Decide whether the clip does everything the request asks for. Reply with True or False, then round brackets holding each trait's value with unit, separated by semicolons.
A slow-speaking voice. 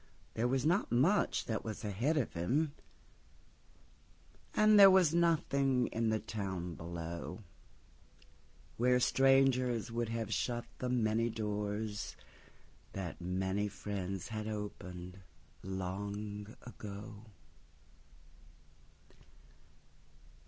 True (85 wpm)